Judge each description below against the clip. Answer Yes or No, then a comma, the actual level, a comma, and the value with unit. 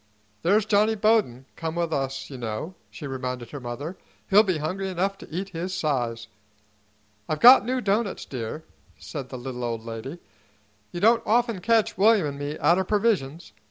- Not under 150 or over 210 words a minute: Yes, average, 175 wpm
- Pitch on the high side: No, medium, 165 Hz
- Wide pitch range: Yes, wide, 7.3 semitones